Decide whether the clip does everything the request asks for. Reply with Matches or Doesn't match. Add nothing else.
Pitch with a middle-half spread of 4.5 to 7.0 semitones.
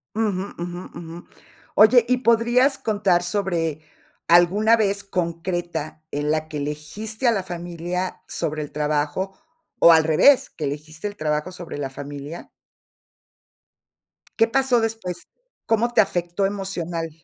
Matches